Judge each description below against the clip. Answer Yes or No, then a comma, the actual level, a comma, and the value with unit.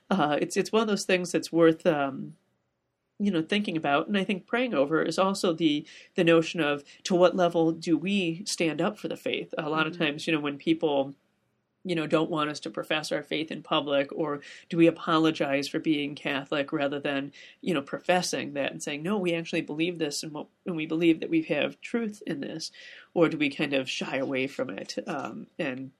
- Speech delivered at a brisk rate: Yes, fast, 215 wpm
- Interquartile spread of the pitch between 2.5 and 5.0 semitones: Yes, average, 3.2 semitones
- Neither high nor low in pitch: Yes, medium, 165 Hz